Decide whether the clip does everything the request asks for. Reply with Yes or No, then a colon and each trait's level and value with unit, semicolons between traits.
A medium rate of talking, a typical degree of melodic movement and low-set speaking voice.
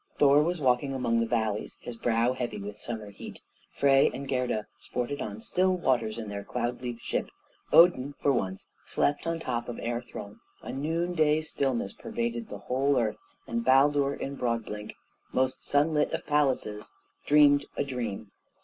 Yes: average, 170 wpm; average, 3.7 semitones; low, 125 Hz